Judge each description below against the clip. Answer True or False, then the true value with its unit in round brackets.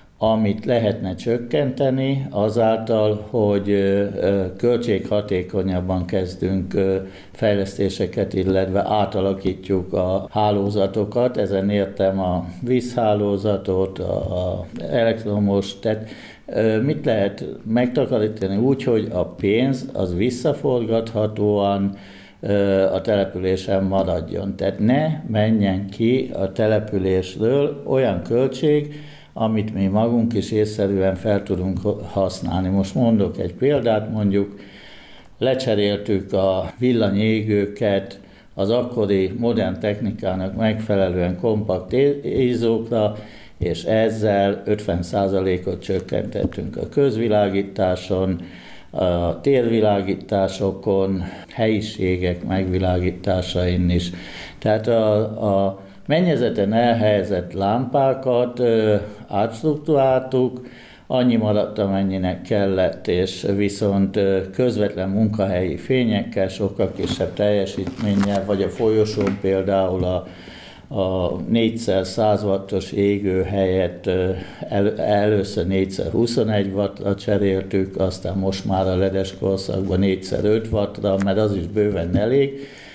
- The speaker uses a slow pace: True (90 wpm)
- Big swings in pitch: False (2.5 semitones)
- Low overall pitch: True (100 Hz)